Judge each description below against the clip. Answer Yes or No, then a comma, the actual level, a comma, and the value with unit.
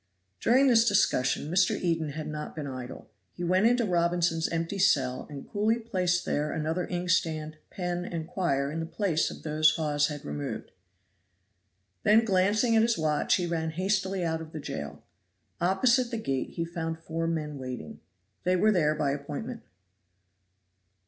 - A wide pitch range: No, average, 3.9 semitones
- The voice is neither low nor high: Yes, medium, 170 Hz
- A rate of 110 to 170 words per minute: Yes, average, 160 wpm